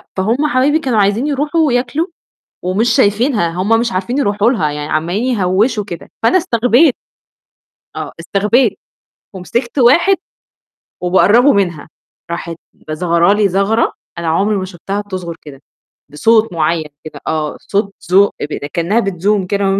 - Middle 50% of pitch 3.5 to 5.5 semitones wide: Yes, average, 5.2 semitones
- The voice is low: No, high, 200 Hz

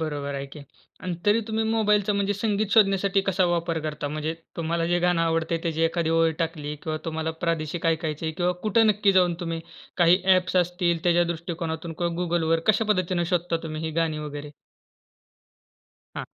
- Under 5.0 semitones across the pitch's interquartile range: Yes, narrow, 2.5 semitones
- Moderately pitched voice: Yes, medium, 170 Hz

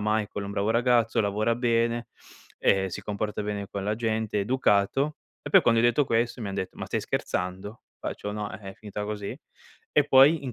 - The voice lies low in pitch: Yes, low, 110 Hz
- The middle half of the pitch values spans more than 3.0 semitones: No, average, 2.7 semitones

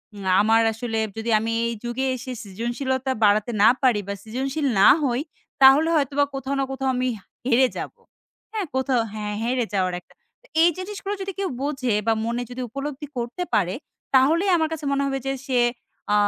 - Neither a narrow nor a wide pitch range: Yes, average, 3.5 semitones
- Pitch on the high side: Yes, very high, 260 Hz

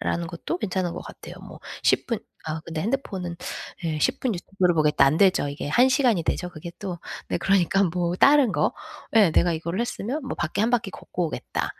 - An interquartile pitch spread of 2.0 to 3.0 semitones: No, average, 5.1 semitones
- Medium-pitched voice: Yes, medium, 180 Hz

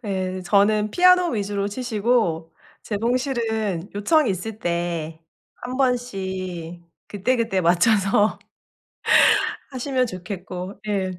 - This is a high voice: Yes, high, 205 Hz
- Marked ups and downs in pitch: No, average, 4.5 semitones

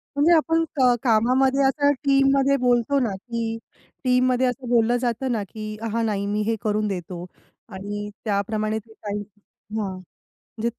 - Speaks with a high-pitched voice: Yes, high, 230 Hz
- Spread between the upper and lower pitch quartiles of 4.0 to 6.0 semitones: No, average, 3.6 semitones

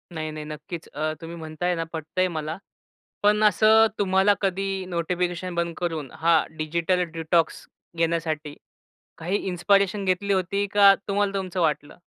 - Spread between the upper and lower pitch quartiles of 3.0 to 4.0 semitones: Yes, average, 3.3 semitones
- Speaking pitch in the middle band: Yes, medium, 175 Hz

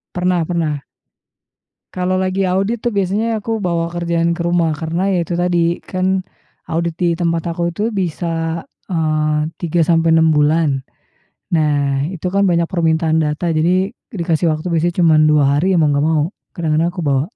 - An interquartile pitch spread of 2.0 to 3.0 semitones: Yes, narrow, 2.4 semitones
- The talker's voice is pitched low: No, medium, 170 Hz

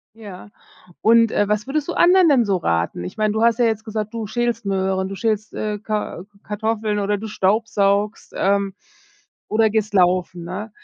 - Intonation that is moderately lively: No, narrow, 2.2 semitones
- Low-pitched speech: No, high, 210 Hz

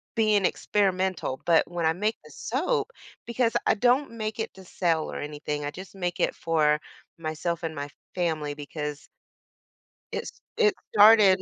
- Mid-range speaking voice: Yes, medium, 175 Hz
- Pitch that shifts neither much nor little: No, wide, 5.8 semitones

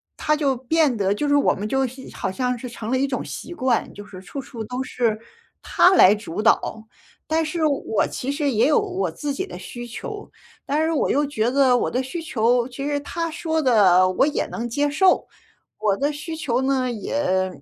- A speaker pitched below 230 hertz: No, very high, 260 Hz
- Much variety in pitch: No, average, 4.5 semitones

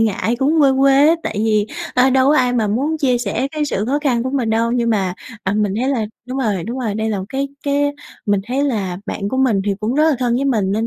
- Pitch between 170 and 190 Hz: No, high, 245 Hz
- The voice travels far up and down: No, average, 4.2 semitones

